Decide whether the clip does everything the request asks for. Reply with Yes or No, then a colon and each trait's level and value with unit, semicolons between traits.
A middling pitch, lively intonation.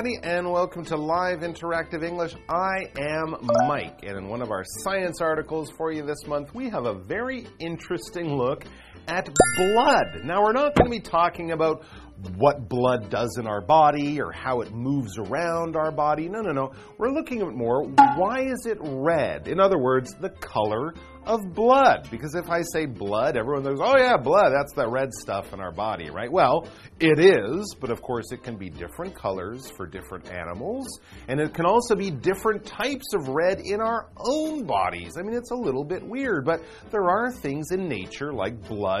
Yes: medium, 160 Hz; wide, 7.5 semitones